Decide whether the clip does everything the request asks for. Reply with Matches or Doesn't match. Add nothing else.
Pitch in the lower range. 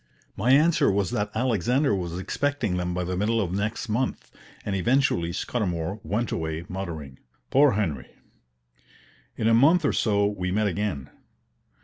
Matches